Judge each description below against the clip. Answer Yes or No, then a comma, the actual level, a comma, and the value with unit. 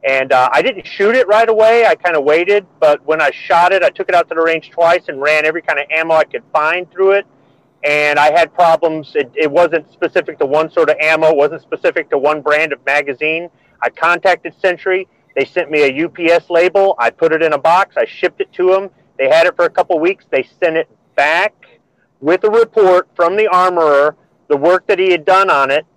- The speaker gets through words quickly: Yes, fast, 235 wpm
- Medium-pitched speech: Yes, medium, 170 Hz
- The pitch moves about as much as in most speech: Yes, average, 3.9 semitones